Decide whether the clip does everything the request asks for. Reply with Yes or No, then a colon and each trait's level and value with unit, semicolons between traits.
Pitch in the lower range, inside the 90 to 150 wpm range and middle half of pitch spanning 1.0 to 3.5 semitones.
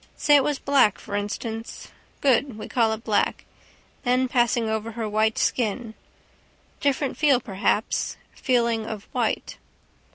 No: high, 230 Hz; slow, 135 wpm; average, 3.0 semitones